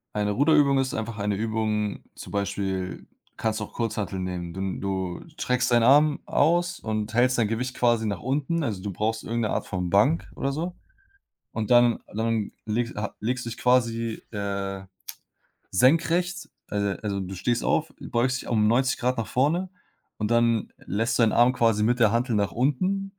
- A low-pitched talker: Yes, low, 115 Hz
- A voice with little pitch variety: No, average, 3.7 semitones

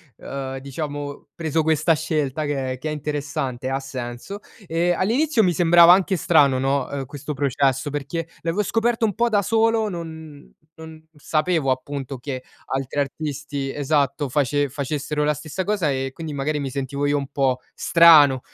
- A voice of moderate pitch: Yes, medium, 145 Hz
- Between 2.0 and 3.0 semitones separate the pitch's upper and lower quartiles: No, average, 3.4 semitones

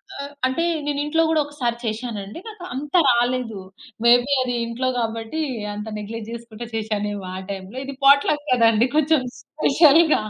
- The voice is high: Yes, high, 245 Hz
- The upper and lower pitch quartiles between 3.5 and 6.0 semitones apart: Yes, average, 4.4 semitones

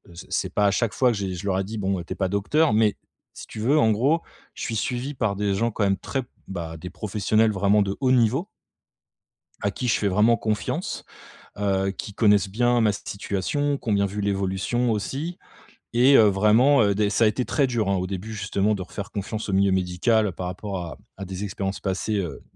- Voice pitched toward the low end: Yes, low, 105 Hz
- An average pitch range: Yes, average, 3.0 semitones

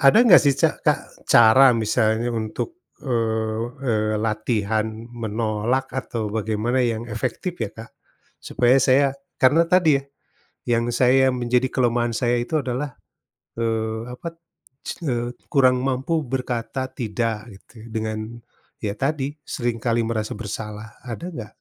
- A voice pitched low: Yes, low, 120 Hz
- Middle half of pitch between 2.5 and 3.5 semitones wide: Yes, average, 3.0 semitones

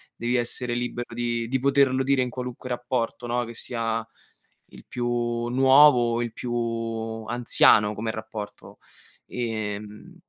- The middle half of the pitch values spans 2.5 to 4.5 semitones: No, narrow, 1.8 semitones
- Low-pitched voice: Yes, low, 120 Hz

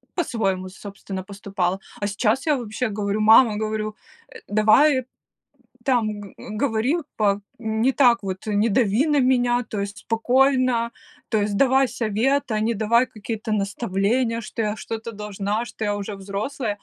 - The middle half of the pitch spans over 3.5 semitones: No, average, 3.1 semitones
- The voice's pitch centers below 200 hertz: No, high, 220 Hz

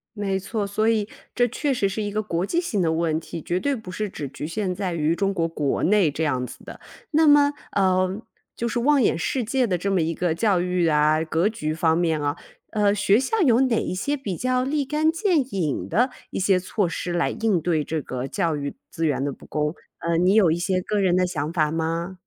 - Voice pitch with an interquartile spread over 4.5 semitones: Yes, average, 5.1 semitones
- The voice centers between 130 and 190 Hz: Yes, medium, 185 Hz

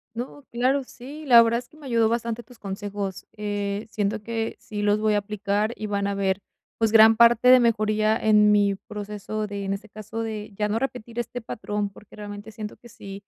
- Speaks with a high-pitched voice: Yes, high, 215 Hz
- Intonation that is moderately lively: No, narrow, 2.1 semitones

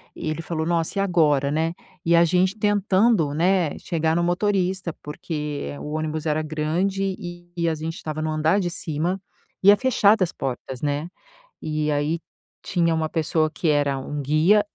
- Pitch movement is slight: No, average, 3.2 semitones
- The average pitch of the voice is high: No, medium, 160 Hz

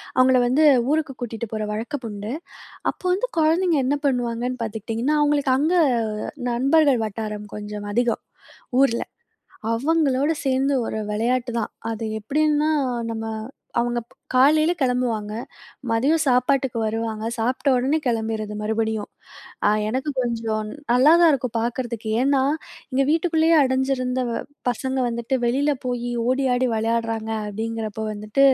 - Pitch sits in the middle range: No, high, 245 Hz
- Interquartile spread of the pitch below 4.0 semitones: Yes, average, 3.6 semitones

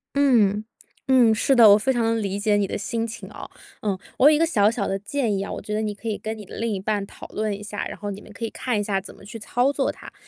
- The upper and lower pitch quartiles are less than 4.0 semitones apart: Yes, narrow, 2.5 semitones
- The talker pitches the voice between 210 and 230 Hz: Yes, high, 215 Hz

